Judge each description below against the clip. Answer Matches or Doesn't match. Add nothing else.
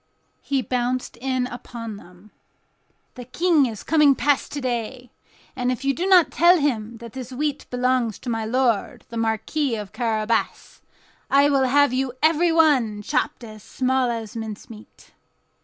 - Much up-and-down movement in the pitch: Doesn't match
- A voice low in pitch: Doesn't match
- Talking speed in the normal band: Matches